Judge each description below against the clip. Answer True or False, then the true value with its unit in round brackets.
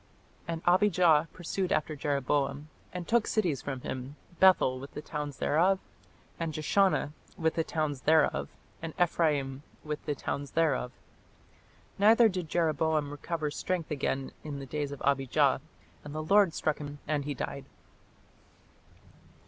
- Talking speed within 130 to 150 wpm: True (140 wpm)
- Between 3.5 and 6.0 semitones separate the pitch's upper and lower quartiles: False (3.0 semitones)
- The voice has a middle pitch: True (155 Hz)